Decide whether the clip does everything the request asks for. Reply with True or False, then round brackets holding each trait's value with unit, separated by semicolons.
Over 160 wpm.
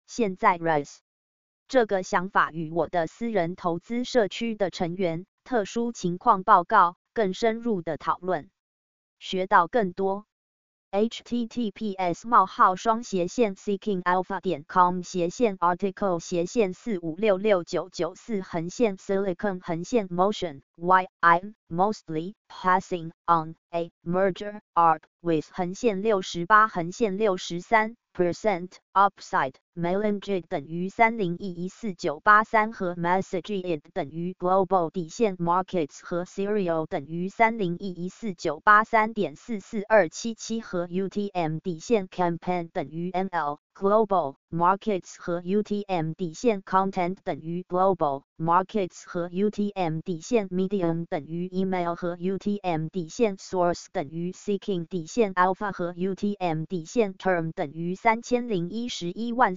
False (155 wpm)